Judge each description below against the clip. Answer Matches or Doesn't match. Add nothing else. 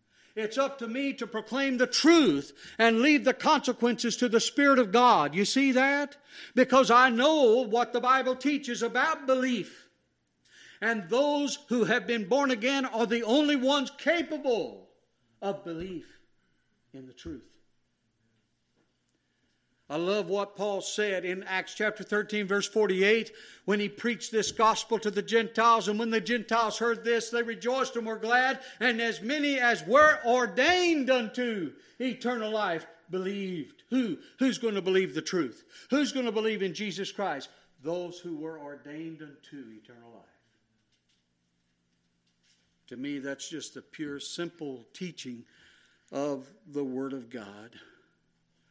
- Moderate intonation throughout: Doesn't match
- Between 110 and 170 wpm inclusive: Matches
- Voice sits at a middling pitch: Doesn't match